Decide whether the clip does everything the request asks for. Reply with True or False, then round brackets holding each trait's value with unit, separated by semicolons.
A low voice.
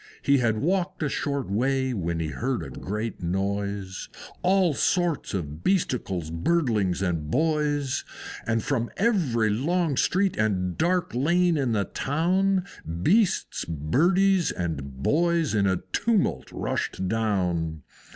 True (125 Hz)